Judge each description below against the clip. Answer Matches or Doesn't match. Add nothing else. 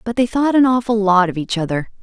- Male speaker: Doesn't match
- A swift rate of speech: Matches